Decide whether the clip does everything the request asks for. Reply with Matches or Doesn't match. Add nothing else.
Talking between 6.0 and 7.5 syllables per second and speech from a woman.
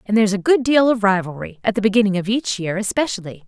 Matches